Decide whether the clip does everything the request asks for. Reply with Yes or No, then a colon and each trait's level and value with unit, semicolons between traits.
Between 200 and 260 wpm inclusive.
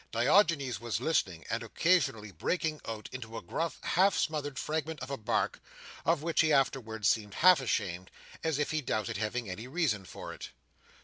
No: average, 175 wpm